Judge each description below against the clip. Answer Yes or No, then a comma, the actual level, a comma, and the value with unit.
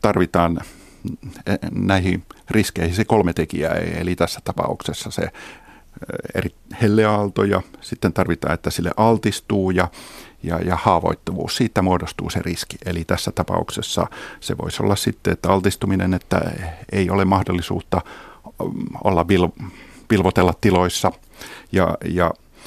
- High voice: No, very low, 90 Hz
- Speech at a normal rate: Yes, average, 120 wpm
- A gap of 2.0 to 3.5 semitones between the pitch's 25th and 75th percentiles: Yes, narrow, 2.5 semitones